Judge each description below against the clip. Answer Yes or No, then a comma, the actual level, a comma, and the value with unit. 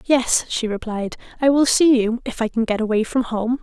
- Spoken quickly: Yes, fast, 230 wpm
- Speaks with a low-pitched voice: No, high, 235 Hz